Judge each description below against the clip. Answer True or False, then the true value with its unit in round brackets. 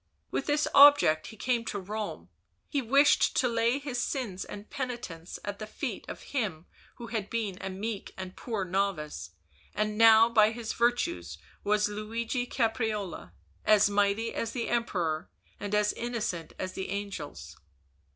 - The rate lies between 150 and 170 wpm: True (155 wpm)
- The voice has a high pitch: True (215 Hz)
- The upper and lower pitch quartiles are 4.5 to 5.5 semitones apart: False (3.2 semitones)